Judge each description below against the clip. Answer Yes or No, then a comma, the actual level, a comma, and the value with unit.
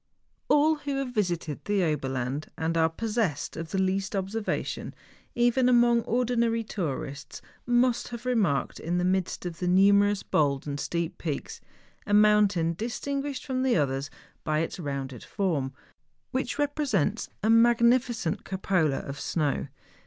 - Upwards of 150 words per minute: No, average, 145 wpm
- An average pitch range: No, wide, 6.9 semitones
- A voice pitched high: Yes, high, 195 Hz